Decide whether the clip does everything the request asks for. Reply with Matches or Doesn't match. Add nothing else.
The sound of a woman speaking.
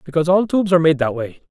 Doesn't match